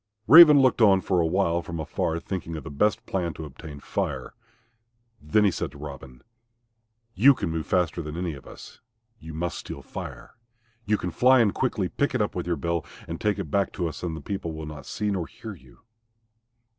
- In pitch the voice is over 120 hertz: No, very low, 85 Hz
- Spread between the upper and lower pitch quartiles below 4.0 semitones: No, average, 4.3 semitones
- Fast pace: Yes, fast, 210 wpm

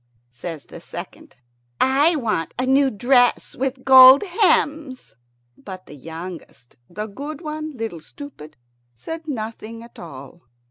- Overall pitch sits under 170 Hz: No, high, 245 Hz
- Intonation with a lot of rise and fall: Yes, wide, 8.2 semitones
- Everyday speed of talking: No, slow, 130 wpm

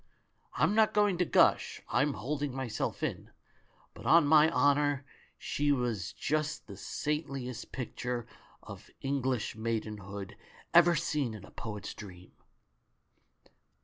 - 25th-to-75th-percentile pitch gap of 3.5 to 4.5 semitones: No, average, 5.2 semitones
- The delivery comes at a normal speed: No, slow, 130 wpm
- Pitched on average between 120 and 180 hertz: Yes, low, 135 Hz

